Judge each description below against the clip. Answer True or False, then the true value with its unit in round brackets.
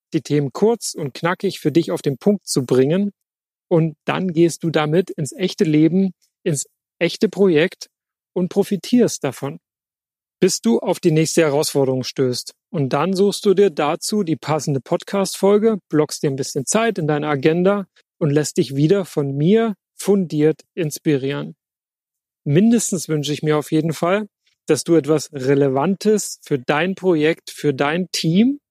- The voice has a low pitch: False (165 Hz)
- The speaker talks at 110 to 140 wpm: False (155 wpm)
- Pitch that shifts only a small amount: False (4.5 semitones)